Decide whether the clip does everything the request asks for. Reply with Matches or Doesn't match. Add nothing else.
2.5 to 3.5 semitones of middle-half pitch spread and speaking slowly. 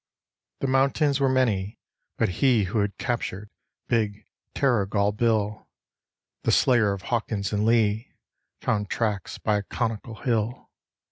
Matches